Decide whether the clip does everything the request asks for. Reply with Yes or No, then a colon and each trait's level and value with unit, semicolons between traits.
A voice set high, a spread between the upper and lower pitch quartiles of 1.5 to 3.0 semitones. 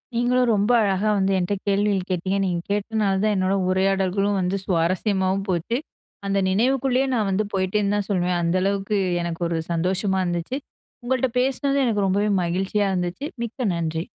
Yes: high, 195 Hz; narrow, 2.5 semitones